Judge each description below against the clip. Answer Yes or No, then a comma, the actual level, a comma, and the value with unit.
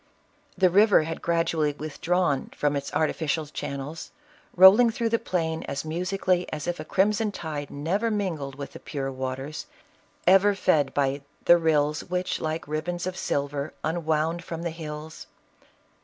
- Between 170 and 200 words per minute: No, average, 155 wpm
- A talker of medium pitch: Yes, medium, 160 Hz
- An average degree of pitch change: Yes, average, 3.6 semitones